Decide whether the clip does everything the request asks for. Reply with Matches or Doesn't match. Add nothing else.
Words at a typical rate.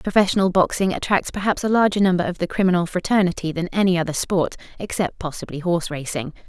Matches